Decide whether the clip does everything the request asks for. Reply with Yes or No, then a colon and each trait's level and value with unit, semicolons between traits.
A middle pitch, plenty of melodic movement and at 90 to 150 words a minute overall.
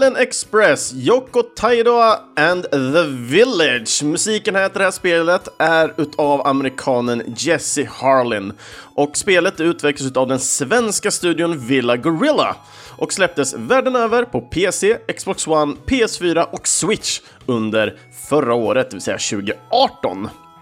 Yes: medium, 165 Hz; wide, 7.5 semitones; average, 130 wpm